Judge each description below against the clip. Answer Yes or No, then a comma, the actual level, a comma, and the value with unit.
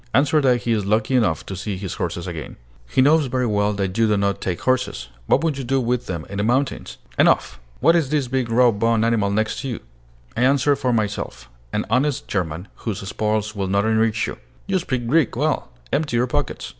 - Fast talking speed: Yes, fast, 215 wpm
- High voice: No, low, 115 Hz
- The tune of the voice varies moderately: Yes, average, 4.6 semitones